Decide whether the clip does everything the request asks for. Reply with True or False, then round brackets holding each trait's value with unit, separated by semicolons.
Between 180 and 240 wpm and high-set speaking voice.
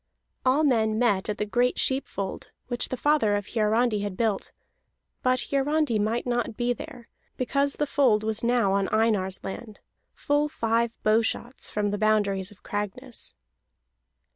False (155 wpm; 225 Hz)